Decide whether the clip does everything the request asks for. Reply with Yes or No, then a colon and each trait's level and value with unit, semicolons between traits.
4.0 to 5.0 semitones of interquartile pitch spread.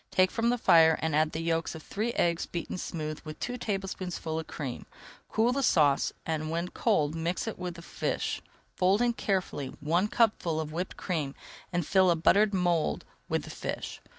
No: average, 3.6 semitones